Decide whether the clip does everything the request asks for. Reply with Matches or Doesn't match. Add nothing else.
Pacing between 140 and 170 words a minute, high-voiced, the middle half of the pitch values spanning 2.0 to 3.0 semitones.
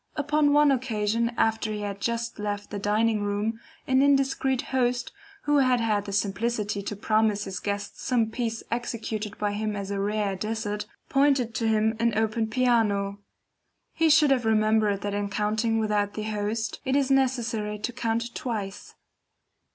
Matches